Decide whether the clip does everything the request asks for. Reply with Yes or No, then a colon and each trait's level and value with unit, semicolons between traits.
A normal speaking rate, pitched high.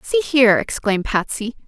Yes: average, 145 wpm; high, 210 Hz